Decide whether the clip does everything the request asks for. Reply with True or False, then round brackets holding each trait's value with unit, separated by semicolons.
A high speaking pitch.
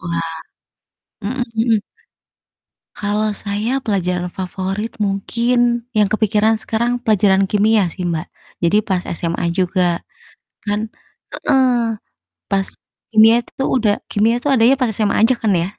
True (210 Hz)